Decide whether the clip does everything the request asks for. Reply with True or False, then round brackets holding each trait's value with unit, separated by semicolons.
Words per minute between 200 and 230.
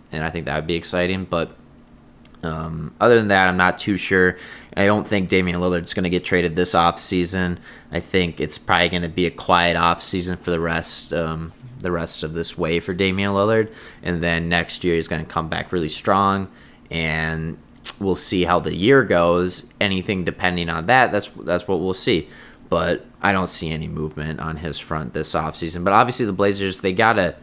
True (205 wpm)